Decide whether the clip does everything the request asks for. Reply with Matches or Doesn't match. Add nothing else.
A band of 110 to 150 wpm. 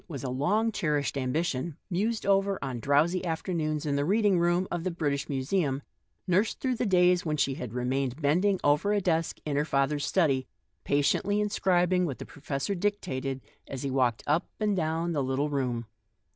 Doesn't match